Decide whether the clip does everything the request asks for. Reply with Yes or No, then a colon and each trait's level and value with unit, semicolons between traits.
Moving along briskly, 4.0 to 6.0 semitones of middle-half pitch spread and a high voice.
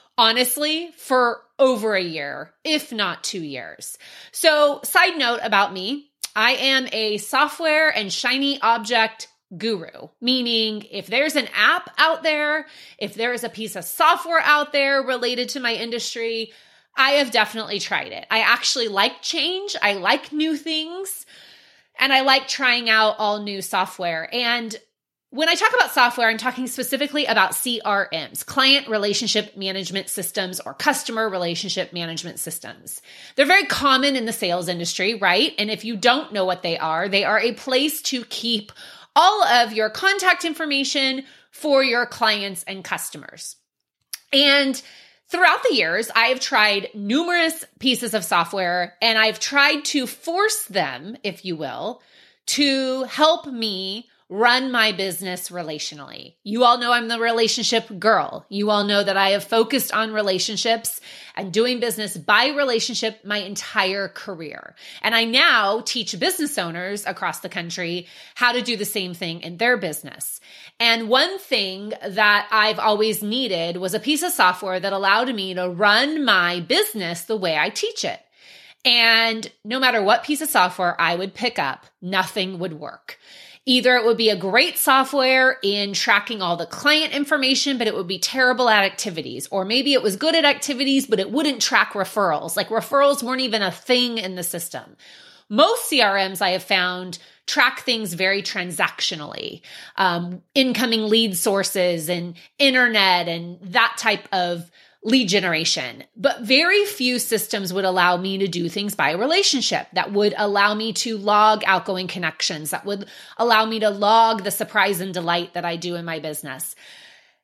No: average, 165 wpm; average, 5.2 semitones; high, 225 Hz